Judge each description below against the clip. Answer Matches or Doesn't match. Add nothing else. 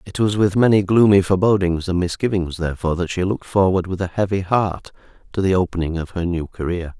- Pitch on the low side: Matches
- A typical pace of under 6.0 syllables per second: Doesn't match